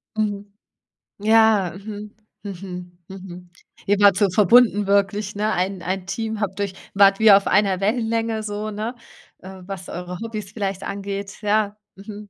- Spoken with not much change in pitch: Yes, narrow, 1.8 semitones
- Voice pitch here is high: Yes, high, 200 Hz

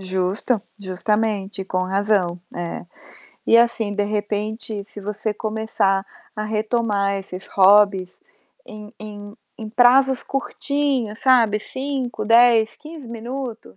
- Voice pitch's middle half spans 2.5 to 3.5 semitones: Yes, average, 2.8 semitones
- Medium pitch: No, high, 215 Hz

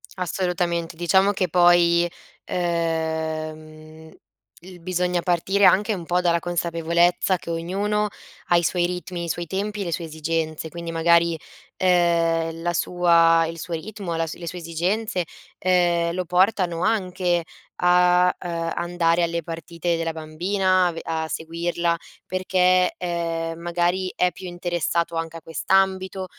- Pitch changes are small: Yes, narrow, 1.5 semitones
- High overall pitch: No, medium, 175 Hz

